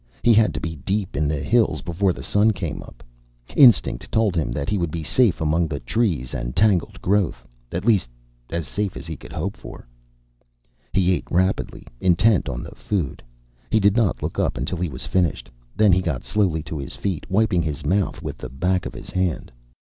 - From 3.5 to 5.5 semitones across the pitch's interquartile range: Yes, average, 4.7 semitones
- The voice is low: Yes, very low, 90 Hz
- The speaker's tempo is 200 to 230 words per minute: Yes, fast, 205 wpm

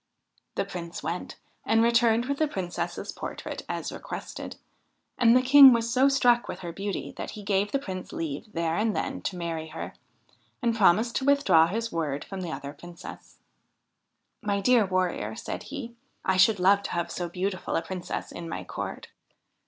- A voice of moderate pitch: No, high, 195 Hz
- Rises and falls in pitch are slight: No, average, 5.3 semitones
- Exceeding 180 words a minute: Yes, average, 190 wpm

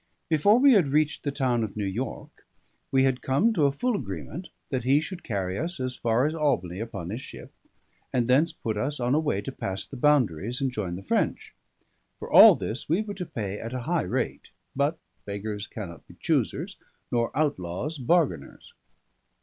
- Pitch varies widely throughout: Yes, wide, 6.4 semitones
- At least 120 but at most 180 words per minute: No, average, 190 wpm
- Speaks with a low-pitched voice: Yes, low, 130 Hz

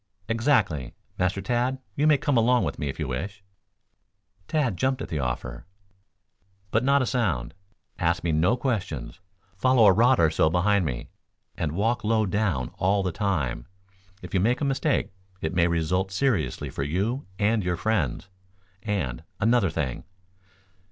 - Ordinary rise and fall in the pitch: No, wide, 6.9 semitones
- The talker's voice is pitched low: Yes, very low, 95 Hz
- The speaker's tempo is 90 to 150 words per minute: No, average, 160 wpm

